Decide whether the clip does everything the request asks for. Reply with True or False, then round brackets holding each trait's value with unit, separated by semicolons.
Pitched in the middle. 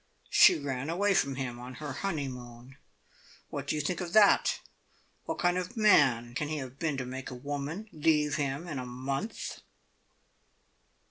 True (145 Hz)